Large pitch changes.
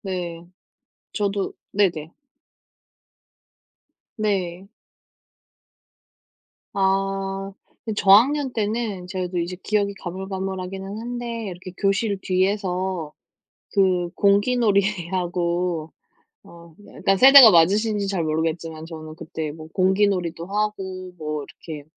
No: average, 2.9 semitones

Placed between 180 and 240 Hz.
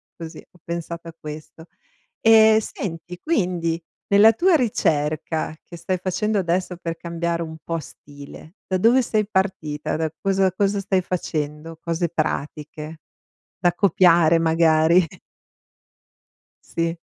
No: medium, 170 Hz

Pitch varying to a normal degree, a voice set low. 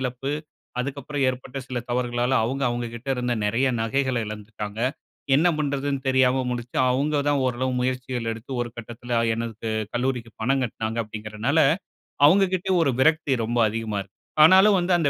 Yes: average, 3.2 semitones; low, 125 Hz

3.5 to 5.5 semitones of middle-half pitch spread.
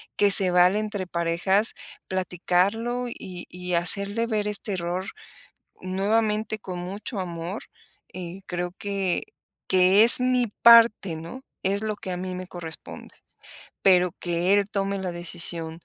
No: average, 2.8 semitones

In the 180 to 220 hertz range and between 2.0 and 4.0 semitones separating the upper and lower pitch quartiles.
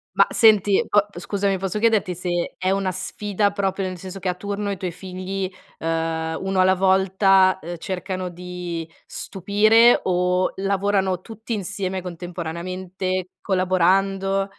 No: high, 190 Hz; narrow, 1.5 semitones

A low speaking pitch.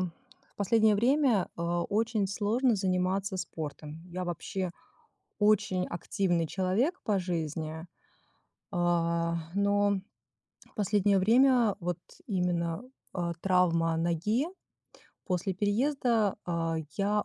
No: high, 190 Hz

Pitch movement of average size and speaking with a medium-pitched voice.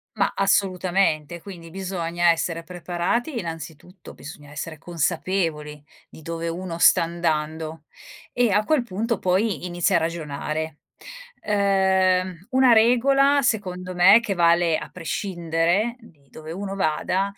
Yes: average, 3.2 semitones; medium, 180 Hz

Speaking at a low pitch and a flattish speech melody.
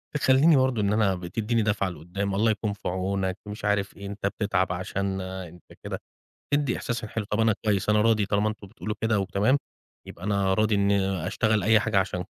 Yes: low, 100 Hz; narrow, 2.2 semitones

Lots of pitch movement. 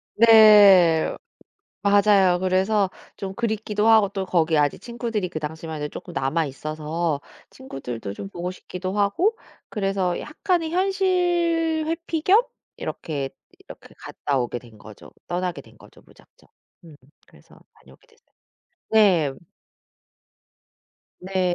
Yes: wide, 6.3 semitones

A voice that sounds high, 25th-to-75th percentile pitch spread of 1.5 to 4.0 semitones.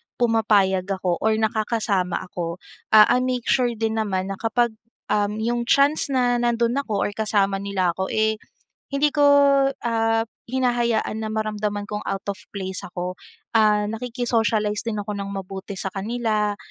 Yes: high, 215 Hz; average, 2.8 semitones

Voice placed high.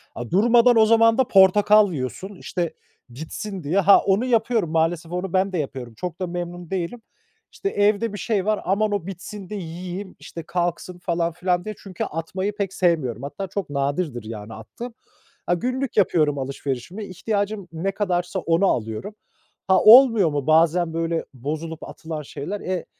No: medium, 180 Hz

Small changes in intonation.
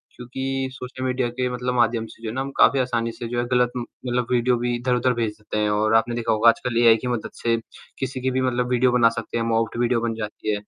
Yes: narrow, 1.5 semitones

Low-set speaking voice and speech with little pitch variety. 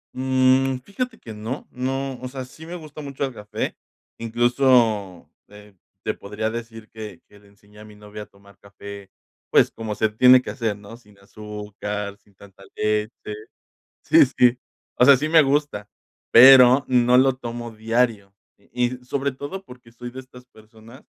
No: low, 115 Hz; average, 3.8 semitones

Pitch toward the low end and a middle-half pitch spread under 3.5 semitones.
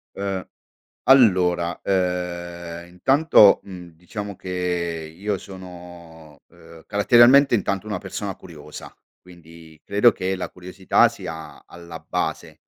Yes: very low, 90 Hz; narrow, 2.5 semitones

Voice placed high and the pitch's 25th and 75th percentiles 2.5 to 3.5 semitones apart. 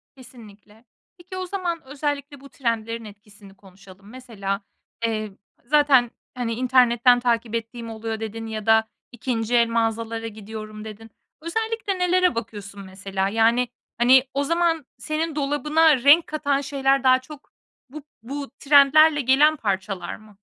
No: high, 240 Hz; average, 4.8 semitones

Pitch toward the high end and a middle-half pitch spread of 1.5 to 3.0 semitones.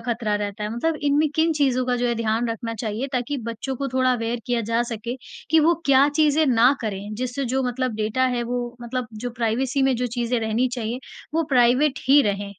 Yes: high, 245 Hz; average, 2.7 semitones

